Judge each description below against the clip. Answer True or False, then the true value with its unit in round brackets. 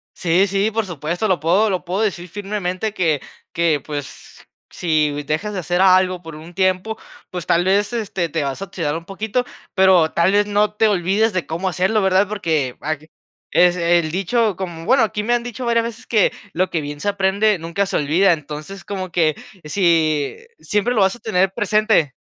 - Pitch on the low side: False (185 Hz)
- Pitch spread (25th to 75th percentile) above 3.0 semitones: True (3.9 semitones)